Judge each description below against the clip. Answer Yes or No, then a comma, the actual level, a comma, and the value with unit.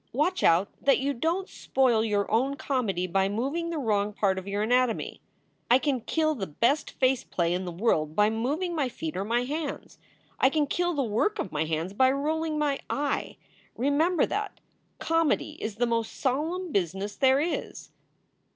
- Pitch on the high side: Yes, very high, 255 Hz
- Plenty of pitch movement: Yes, wide, 6.7 semitones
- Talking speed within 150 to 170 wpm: No, average, 185 wpm